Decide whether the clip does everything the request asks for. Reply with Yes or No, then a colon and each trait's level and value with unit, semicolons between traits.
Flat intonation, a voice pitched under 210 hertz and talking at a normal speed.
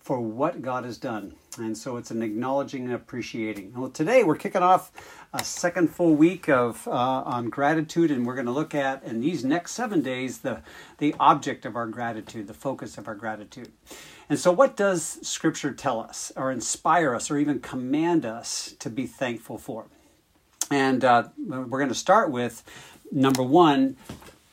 No: average, 4.7 semitones; low, 135 Hz; average, 180 wpm